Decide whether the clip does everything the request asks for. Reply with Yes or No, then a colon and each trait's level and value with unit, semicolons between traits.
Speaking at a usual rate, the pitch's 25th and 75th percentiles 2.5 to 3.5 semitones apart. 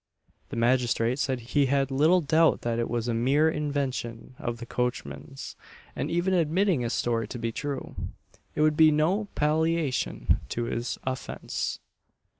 No: average, 155 wpm; average, 4.6 semitones